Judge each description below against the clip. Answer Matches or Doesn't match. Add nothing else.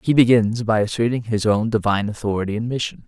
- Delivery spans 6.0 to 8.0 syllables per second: Matches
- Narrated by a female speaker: Doesn't match